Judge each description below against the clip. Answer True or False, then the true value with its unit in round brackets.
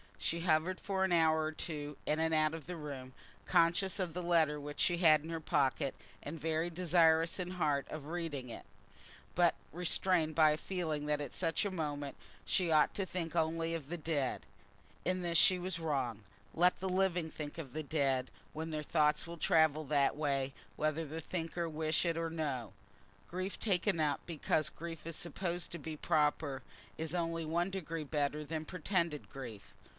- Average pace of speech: True (185 wpm)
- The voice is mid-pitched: True (160 Hz)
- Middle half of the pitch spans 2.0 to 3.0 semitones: True (2.4 semitones)